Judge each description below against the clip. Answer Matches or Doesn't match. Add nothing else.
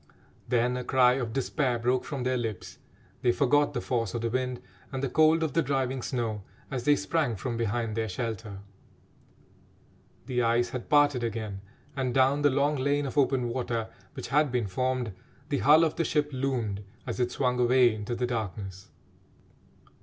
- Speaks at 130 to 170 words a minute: Doesn't match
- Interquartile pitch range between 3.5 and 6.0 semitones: Doesn't match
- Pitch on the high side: Doesn't match